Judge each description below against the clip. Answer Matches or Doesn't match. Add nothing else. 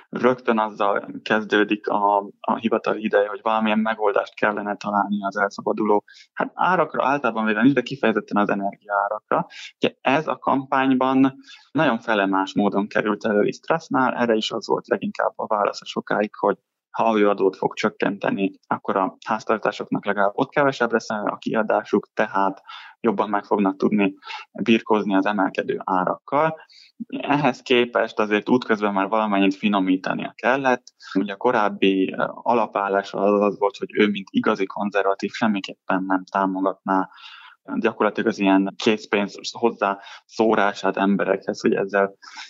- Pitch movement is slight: Matches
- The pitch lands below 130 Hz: Matches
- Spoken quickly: Doesn't match